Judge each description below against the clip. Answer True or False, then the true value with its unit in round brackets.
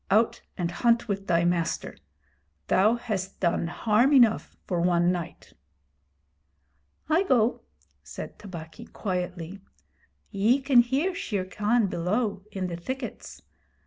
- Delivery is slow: True (120 wpm)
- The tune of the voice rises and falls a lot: False (5.0 semitones)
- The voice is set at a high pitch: True (200 Hz)